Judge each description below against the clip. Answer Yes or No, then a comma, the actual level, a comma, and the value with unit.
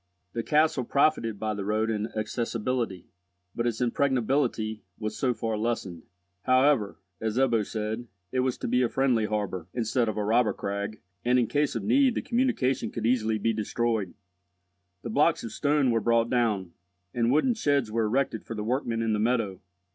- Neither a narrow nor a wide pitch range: Yes, average, 3.1 semitones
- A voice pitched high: No, low, 115 Hz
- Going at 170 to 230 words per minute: Yes, average, 180 wpm